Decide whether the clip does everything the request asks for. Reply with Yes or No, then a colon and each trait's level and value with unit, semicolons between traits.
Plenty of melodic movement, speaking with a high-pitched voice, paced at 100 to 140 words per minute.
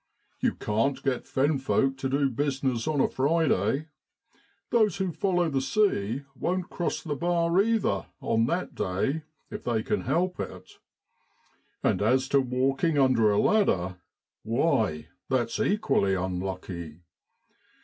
No: wide, 7.1 semitones; low, 135 Hz; slow, 135 wpm